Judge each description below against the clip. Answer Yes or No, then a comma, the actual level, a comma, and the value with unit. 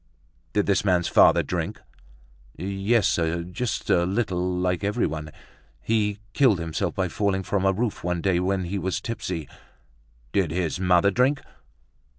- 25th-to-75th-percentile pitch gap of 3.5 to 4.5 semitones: No, narrow, 2.5 semitones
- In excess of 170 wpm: No, average, 150 wpm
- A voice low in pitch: Yes, very low, 95 Hz